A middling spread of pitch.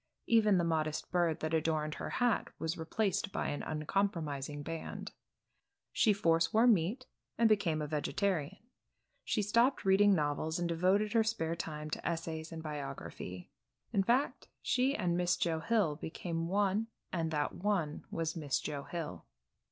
Yes: average, 4.5 semitones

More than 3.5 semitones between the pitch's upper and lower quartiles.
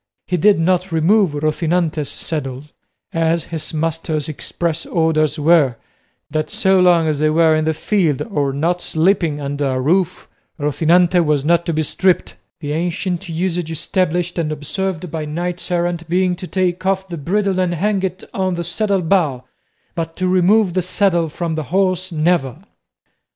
No: average, 2.9 semitones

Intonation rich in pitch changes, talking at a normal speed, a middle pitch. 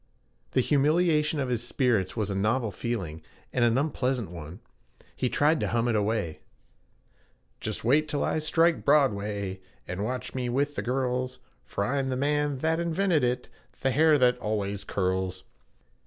No: wide, 5.7 semitones; average, 160 wpm; low, 125 Hz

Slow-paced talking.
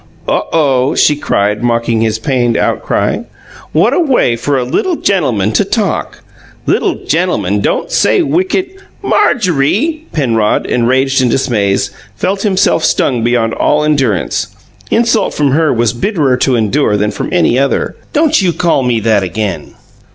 No: average, 150 wpm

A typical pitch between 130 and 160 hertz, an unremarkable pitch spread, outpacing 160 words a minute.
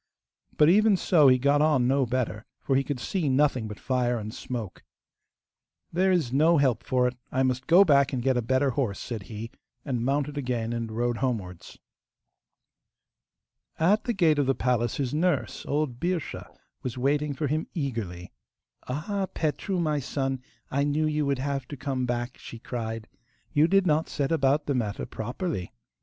Yes: low, 135 Hz; average, 3.8 semitones; average, 180 wpm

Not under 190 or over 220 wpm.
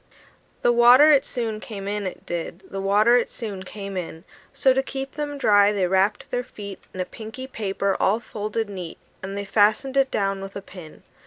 Yes: average, 200 wpm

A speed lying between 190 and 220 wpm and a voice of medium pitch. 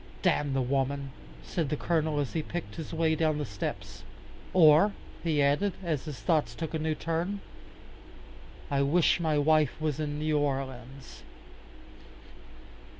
No: average, 150 wpm; medium, 150 Hz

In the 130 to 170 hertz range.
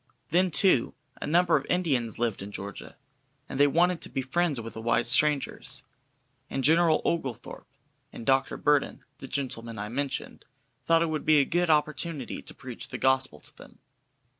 Yes: medium, 140 Hz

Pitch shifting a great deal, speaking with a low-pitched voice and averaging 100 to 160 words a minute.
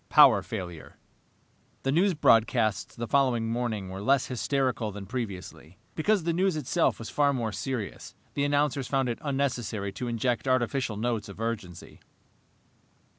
No: average, 4.5 semitones; low, 120 Hz; average, 145 wpm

